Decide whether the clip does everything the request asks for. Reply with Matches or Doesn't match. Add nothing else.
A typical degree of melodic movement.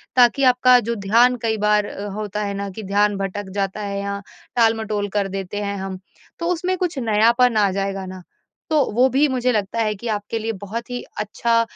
Matches